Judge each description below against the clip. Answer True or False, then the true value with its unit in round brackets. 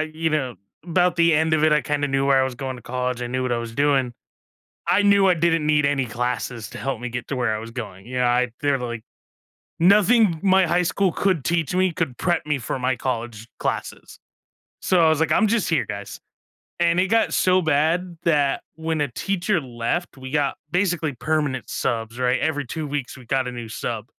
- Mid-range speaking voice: True (145 Hz)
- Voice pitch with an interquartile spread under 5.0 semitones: False (5.3 semitones)